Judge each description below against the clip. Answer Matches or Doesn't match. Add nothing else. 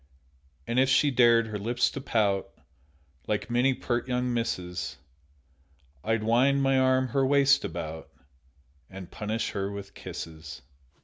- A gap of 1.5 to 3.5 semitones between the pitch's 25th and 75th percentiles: Doesn't match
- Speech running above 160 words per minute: Doesn't match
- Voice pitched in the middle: Doesn't match